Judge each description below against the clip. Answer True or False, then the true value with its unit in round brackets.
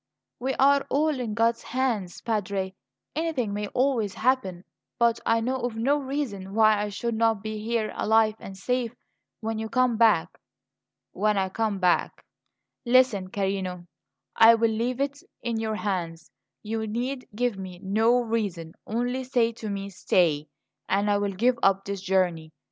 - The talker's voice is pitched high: True (220 Hz)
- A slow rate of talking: False (160 wpm)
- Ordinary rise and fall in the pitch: True (3.8 semitones)